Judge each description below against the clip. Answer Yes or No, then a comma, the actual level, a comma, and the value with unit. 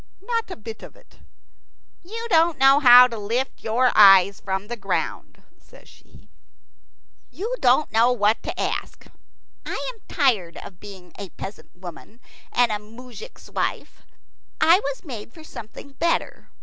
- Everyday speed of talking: Yes, average, 150 wpm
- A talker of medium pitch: No, high, 245 Hz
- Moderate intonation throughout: No, wide, 6.6 semitones